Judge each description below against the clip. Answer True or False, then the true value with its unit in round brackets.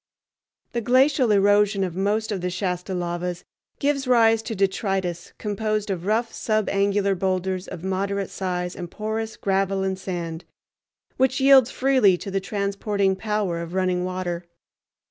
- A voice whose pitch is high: True (195 Hz)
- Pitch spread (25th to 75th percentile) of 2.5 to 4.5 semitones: True (2.9 semitones)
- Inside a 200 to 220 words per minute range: False (145 wpm)